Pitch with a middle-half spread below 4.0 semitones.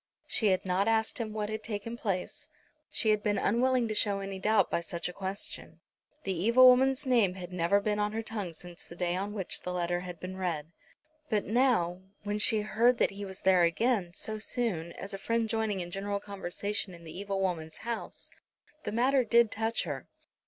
Yes: average, 3.5 semitones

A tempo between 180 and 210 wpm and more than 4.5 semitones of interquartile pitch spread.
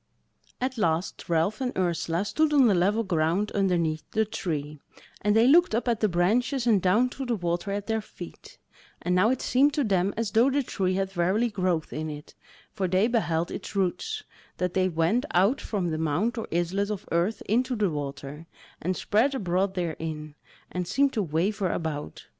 Yes: average, 190 wpm; average, 4.9 semitones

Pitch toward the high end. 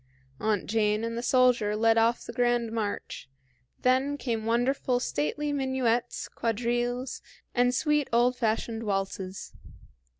Yes: high, 235 Hz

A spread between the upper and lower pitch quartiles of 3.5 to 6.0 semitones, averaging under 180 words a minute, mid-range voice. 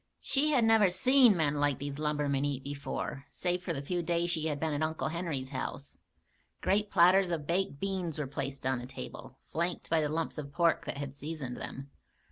No: average, 3.9 semitones; fast, 205 wpm; medium, 155 Hz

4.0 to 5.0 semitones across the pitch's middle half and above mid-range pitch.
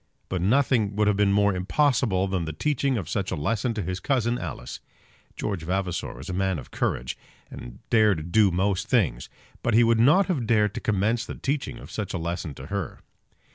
No: average, 4.5 semitones; low, 100 Hz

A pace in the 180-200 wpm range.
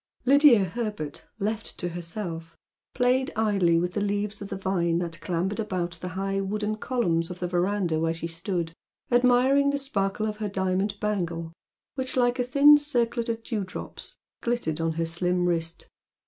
No: average, 165 wpm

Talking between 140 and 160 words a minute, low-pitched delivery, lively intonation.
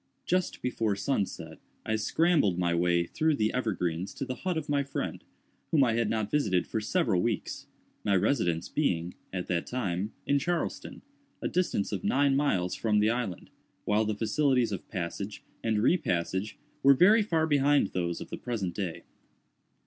No: average, 170 wpm; low, 110 Hz; wide, 7.1 semitones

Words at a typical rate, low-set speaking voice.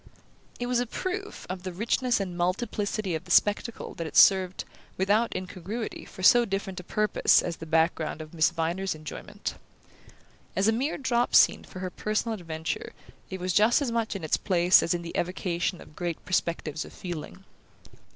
No: average, 180 wpm; medium, 185 Hz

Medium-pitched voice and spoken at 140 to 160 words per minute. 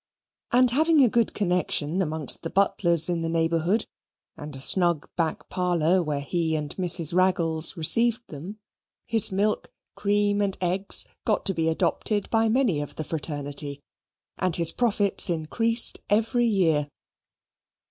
Yes: medium, 180 Hz; average, 145 wpm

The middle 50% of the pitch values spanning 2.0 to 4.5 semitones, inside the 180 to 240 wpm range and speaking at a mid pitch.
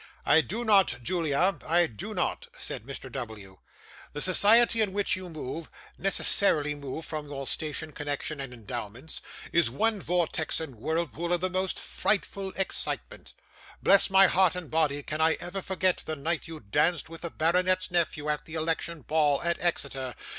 No: average, 4.1 semitones; average, 170 wpm; medium, 160 Hz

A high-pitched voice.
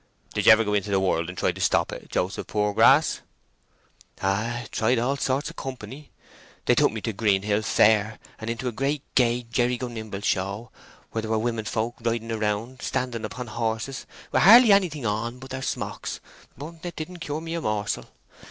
No: low, 115 Hz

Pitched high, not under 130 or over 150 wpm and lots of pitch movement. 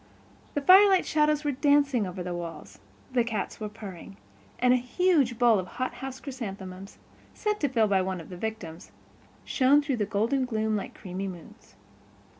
No: high, 225 Hz; average, 170 wpm; wide, 6.4 semitones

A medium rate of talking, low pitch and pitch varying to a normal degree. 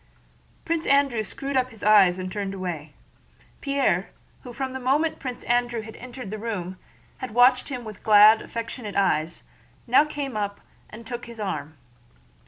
No: average, 160 wpm; high, 230 Hz; average, 4.3 semitones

